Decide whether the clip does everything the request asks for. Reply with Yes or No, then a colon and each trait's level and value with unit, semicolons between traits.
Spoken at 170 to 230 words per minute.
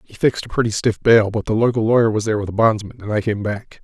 No: fast, 295 wpm